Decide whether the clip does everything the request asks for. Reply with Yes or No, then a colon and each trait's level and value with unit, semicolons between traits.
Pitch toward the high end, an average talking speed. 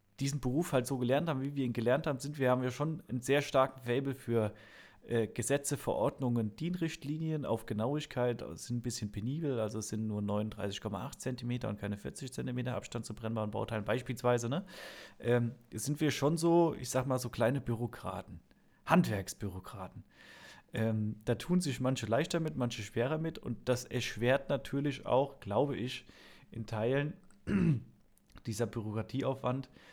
No: low, 125 Hz; average, 160 wpm